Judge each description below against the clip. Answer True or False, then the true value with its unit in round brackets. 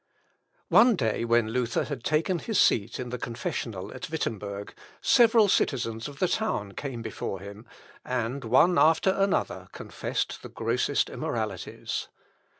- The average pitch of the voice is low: True (125 Hz)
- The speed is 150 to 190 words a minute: False (140 wpm)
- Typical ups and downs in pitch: False (6.9 semitones)